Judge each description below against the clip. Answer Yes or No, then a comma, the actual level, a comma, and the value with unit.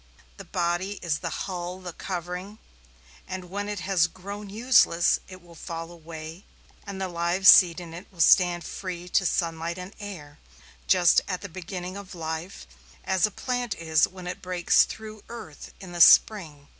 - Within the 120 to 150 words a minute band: No, average, 170 wpm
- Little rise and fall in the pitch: Yes, narrow, 2.3 semitones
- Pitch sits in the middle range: Yes, medium, 180 Hz